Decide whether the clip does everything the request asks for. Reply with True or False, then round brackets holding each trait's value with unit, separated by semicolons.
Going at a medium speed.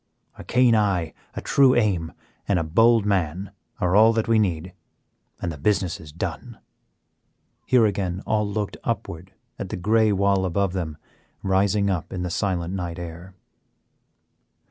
True (155 wpm)